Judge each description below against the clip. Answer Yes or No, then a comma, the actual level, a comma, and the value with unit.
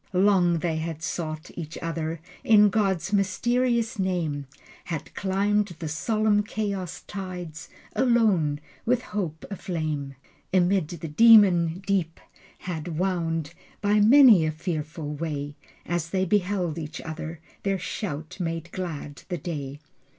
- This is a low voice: No, medium, 175 Hz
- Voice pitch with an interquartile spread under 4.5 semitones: Yes, average, 4.0 semitones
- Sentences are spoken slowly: Yes, slow, 125 wpm